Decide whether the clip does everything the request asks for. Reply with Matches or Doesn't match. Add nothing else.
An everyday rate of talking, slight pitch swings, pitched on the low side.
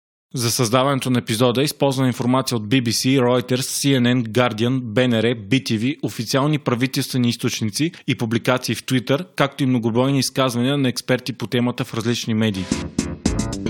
Matches